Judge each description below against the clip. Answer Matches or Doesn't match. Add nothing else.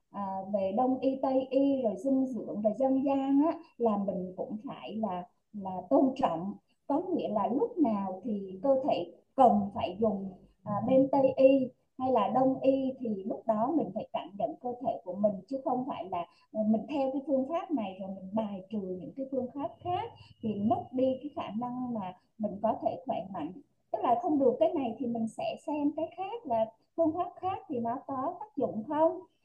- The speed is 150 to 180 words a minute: Doesn't match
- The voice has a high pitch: Matches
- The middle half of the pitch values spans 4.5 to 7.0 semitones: Matches